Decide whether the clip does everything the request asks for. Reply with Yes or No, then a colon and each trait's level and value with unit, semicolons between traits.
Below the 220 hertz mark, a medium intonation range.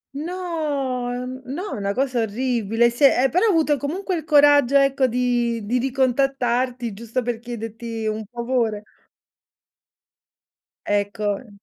No: very high, 250 Hz; average, 3.4 semitones